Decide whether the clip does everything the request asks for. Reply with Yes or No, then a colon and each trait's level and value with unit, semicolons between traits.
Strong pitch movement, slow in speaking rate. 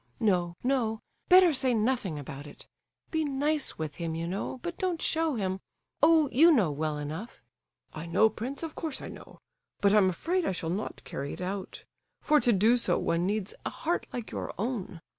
No: wide, 8.6 semitones; average, 190 wpm